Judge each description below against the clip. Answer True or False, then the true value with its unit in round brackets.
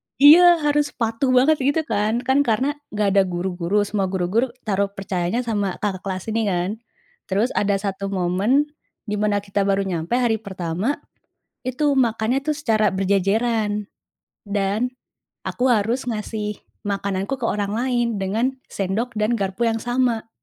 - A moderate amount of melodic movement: True (3.9 semitones)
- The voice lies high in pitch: True (215 Hz)